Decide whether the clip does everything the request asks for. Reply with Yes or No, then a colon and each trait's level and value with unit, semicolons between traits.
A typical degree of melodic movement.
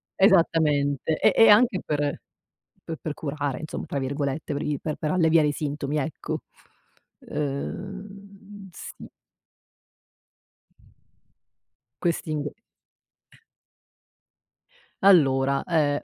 Yes: average, 4.3 semitones